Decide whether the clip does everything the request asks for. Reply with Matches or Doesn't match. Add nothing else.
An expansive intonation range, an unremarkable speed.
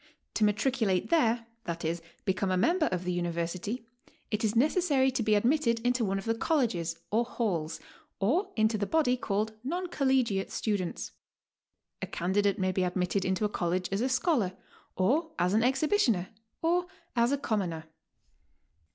Matches